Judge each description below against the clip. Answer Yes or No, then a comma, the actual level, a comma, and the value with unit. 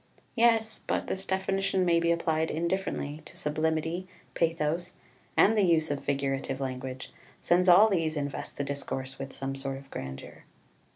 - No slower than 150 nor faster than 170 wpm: Yes, average, 155 wpm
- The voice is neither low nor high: Yes, medium, 160 Hz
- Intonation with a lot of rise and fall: No, average, 4.8 semitones